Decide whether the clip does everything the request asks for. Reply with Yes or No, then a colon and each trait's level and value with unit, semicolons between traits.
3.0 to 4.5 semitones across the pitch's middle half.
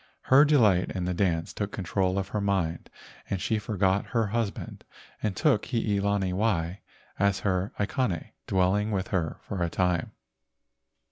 No: narrow, 2.5 semitones